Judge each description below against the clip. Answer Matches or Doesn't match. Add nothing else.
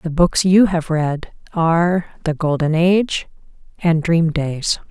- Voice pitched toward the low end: Doesn't match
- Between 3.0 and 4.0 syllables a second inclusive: Matches